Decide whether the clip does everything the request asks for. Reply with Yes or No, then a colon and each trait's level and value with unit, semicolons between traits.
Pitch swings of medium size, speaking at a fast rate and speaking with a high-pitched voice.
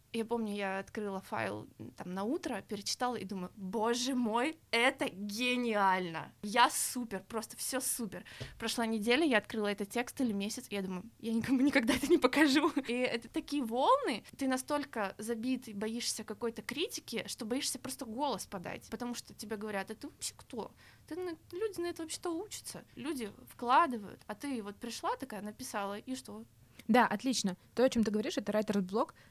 Yes: average, 4.4 semitones; fast, 175 wpm; high, 235 Hz